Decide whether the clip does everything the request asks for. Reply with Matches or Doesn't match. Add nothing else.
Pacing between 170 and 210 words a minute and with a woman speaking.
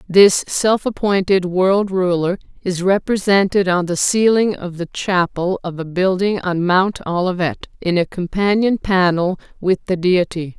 Doesn't match